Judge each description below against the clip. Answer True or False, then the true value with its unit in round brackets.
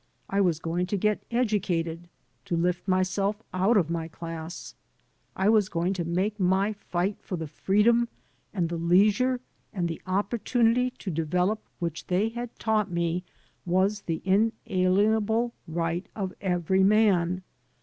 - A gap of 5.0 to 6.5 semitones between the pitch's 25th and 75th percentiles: False (3.6 semitones)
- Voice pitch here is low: False (190 Hz)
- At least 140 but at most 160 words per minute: True (145 wpm)